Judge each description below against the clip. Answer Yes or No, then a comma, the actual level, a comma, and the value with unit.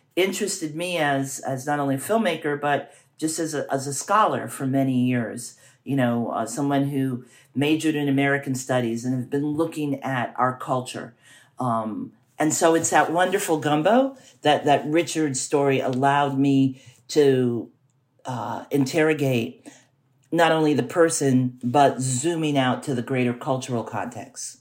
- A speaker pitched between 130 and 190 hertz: Yes, low, 135 Hz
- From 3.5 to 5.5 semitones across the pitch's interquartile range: No, average, 2.8 semitones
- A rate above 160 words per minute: No, average, 150 wpm